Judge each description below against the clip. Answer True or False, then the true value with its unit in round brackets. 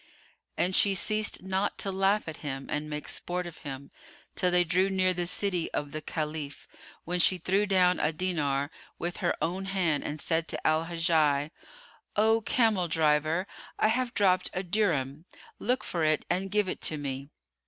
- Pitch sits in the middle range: True (175 Hz)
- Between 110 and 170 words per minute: False (180 wpm)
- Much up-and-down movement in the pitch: False (3.9 semitones)